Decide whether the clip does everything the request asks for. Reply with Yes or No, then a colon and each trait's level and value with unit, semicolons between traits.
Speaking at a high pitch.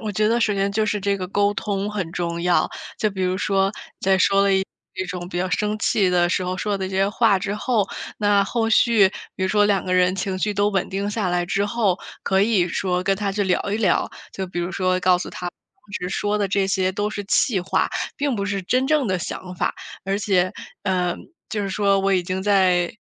Yes: high, 195 Hz